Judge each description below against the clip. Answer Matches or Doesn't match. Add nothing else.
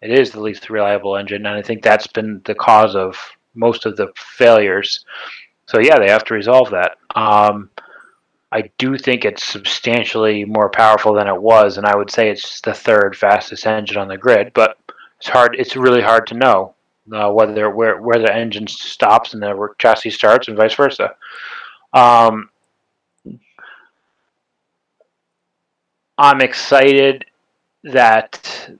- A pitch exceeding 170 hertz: Doesn't match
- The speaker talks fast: Doesn't match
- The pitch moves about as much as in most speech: Doesn't match